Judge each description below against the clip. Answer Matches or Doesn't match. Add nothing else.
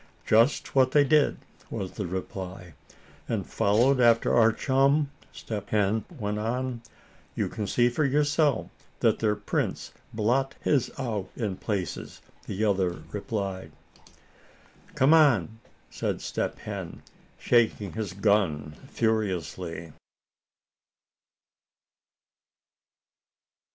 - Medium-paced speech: Doesn't match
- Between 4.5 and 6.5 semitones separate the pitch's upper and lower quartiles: Matches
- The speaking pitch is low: Matches